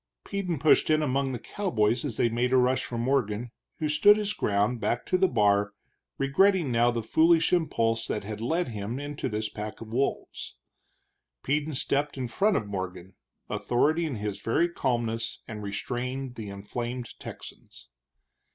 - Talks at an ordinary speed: Yes, average, 165 wpm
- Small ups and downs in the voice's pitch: No, wide, 5.5 semitones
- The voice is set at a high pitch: No, low, 125 Hz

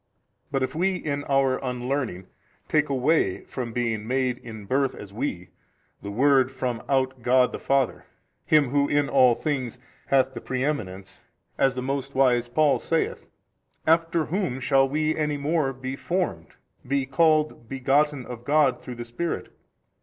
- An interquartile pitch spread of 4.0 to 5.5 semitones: No, average, 2.9 semitones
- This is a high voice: No, low, 135 Hz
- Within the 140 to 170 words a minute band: Yes, average, 155 wpm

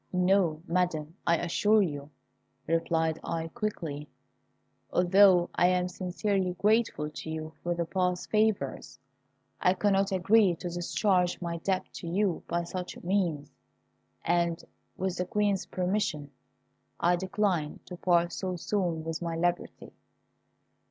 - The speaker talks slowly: Yes, slow, 125 wpm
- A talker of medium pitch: Yes, medium, 175 Hz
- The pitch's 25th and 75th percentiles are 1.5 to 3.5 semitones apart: Yes, narrow, 2.5 semitones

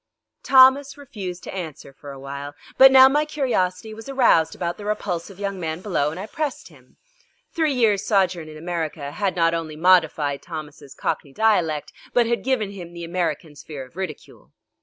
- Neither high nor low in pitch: Yes, medium, 180 Hz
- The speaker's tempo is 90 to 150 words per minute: No, average, 180 wpm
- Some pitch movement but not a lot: No, wide, 5.9 semitones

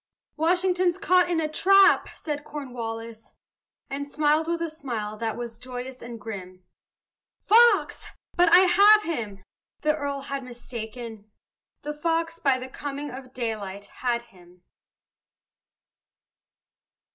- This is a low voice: No, very high, 275 Hz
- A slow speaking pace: Yes, slow, 120 wpm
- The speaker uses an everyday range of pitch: No, wide, 6.2 semitones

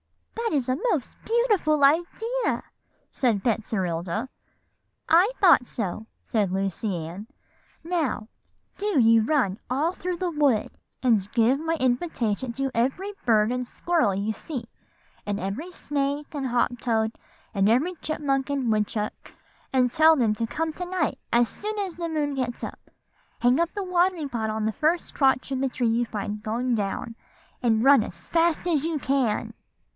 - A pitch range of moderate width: No, wide, 6.5 semitones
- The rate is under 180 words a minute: Yes, average, 160 wpm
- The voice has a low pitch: No, very high, 255 Hz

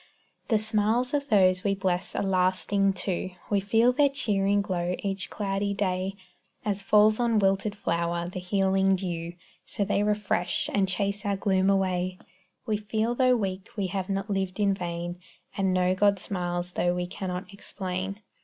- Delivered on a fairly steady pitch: Yes, narrow, 2.0 semitones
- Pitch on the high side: Yes, high, 195 Hz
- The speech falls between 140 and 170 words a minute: Yes, average, 165 wpm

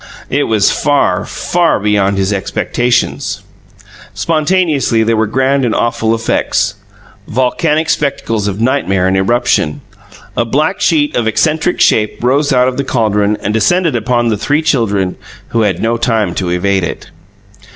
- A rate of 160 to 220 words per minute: No, average, 150 wpm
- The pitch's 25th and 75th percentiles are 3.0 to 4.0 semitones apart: No, average, 5.3 semitones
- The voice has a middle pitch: No, low, 115 Hz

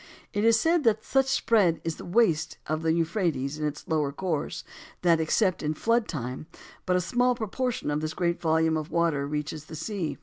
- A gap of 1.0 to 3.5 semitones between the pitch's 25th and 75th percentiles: No, wide, 5.6 semitones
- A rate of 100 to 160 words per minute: No, fast, 205 wpm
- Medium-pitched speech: Yes, medium, 165 Hz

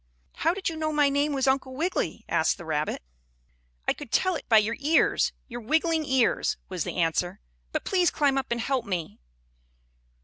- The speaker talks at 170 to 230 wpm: Yes, average, 190 wpm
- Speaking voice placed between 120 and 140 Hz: No, very high, 270 Hz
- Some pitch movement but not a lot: No, wide, 6.1 semitones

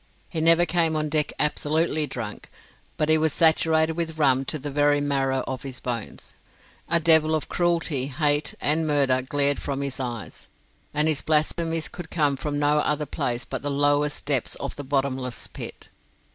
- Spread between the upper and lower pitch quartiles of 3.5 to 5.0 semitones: No, narrow, 2.5 semitones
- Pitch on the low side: No, medium, 145 Hz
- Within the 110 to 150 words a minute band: No, average, 175 wpm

